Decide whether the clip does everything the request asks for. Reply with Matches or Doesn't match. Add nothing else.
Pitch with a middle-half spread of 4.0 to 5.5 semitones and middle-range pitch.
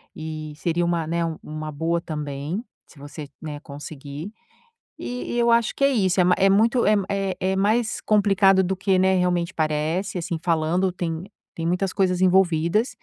Doesn't match